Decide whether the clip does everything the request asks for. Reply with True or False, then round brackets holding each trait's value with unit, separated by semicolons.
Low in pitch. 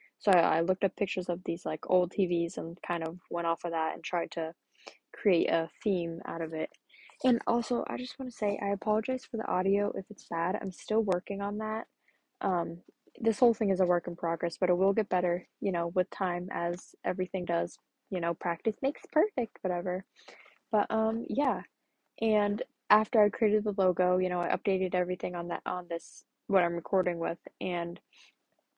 False (185 Hz)